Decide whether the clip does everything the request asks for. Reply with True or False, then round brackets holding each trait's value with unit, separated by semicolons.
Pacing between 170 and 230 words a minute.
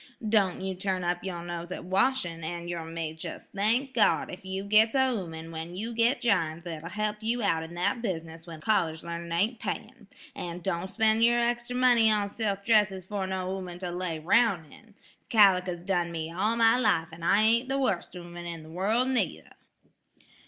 True (195 wpm)